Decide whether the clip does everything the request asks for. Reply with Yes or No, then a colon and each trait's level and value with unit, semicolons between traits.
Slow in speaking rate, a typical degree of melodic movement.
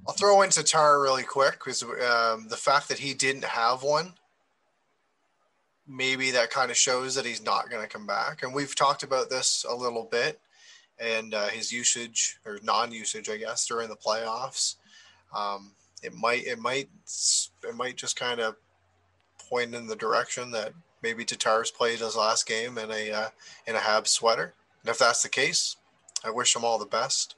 No: average, 185 wpm; average, 3.2 semitones